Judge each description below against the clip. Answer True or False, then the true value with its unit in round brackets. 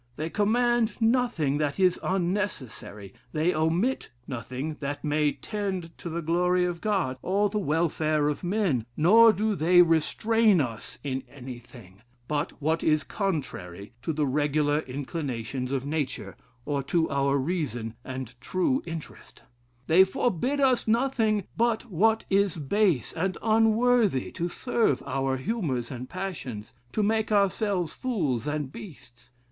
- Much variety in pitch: True (7.0 semitones)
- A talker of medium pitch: True (165 Hz)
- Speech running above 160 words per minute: False (140 wpm)